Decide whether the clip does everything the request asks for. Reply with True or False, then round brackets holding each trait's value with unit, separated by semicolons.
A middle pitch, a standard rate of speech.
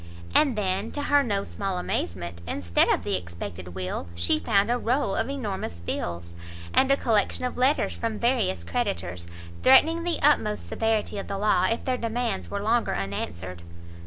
False (200 Hz; 170 wpm)